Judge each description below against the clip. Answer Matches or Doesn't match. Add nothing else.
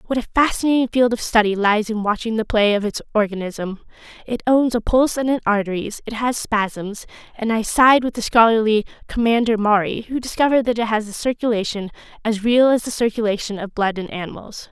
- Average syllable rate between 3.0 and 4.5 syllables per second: Doesn't match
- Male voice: Doesn't match